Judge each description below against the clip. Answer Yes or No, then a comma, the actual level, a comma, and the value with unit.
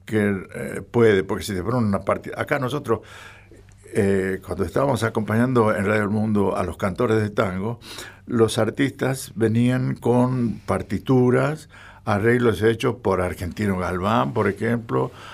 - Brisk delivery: No, average, 140 wpm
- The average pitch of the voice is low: Yes, low, 110 Hz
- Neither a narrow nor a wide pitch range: Yes, average, 3.2 semitones